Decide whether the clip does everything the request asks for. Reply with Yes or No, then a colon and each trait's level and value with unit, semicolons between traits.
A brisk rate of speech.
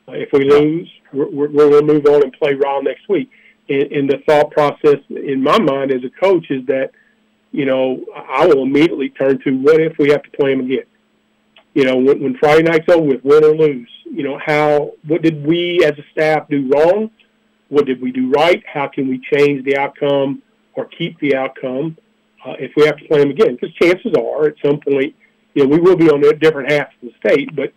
Yes: fast, 230 wpm